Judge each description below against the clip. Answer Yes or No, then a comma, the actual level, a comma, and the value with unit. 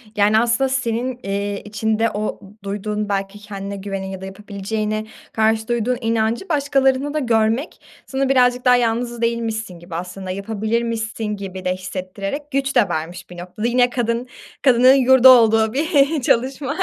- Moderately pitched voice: No, high, 225 Hz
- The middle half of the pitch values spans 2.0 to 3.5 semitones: No, average, 3.9 semitones